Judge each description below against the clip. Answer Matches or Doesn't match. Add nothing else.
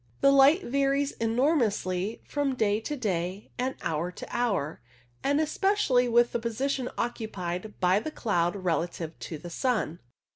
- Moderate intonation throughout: Doesn't match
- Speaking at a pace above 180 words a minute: Doesn't match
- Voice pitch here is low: Doesn't match